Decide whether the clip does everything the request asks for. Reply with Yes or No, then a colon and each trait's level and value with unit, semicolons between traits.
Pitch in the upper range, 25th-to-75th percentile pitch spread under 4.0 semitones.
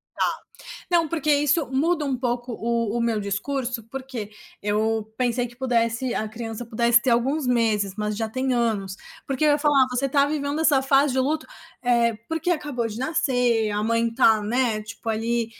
Yes: high, 240 Hz; average, 3.3 semitones